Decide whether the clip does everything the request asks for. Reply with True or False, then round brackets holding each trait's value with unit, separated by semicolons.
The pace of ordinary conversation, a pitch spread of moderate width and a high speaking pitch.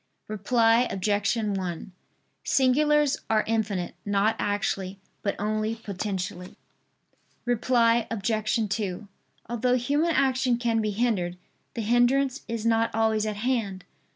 False (115 wpm; 3.1 semitones; 220 Hz)